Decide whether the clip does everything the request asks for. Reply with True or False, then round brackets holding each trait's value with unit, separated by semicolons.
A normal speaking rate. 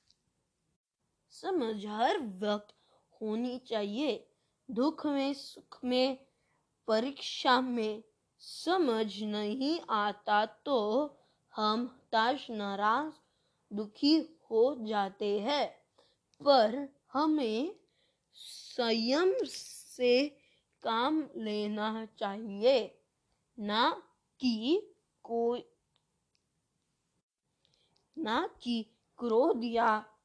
False (70 wpm)